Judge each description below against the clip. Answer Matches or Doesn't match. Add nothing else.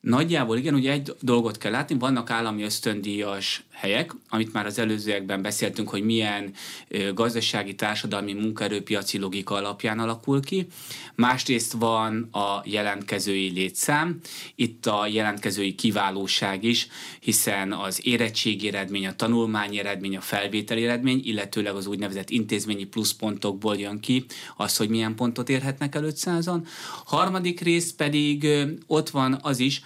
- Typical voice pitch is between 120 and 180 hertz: Doesn't match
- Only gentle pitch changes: Doesn't match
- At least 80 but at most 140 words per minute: Matches